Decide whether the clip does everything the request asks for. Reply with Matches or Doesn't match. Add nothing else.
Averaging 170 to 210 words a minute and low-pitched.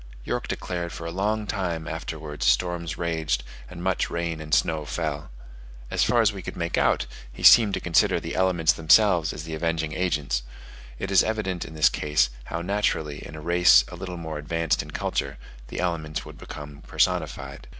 Matches